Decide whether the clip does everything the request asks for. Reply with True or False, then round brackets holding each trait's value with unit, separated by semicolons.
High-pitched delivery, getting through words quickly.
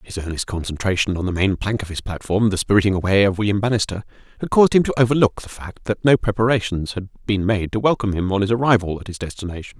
False (100 Hz; 235 wpm)